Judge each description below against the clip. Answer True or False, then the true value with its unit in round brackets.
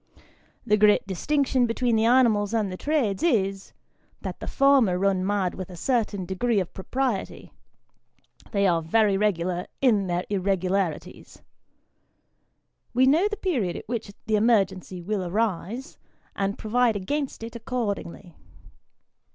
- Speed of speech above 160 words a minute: False (135 wpm)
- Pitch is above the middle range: True (205 Hz)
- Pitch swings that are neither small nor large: True (4.3 semitones)